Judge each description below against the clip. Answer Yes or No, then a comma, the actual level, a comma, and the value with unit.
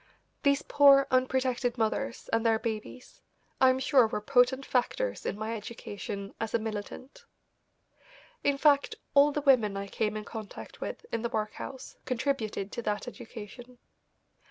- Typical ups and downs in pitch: Yes, average, 3.8 semitones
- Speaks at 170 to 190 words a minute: No, average, 150 wpm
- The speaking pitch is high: Yes, high, 245 Hz